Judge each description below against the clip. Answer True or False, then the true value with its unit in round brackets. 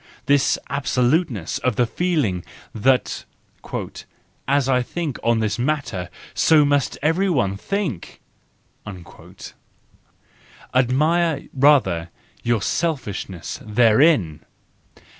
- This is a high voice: False (130 Hz)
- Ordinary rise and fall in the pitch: False (5.8 semitones)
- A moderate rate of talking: False (85 wpm)